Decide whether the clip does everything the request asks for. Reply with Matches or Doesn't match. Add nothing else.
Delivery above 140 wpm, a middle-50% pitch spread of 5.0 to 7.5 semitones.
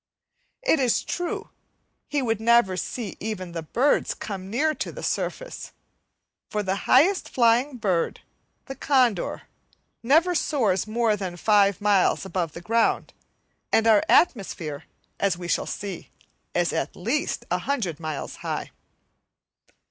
Doesn't match